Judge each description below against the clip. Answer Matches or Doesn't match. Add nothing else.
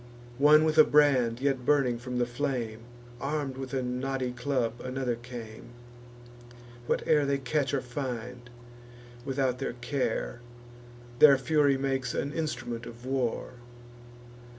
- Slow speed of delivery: Matches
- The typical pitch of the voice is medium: Doesn't match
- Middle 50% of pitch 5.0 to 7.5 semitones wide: Doesn't match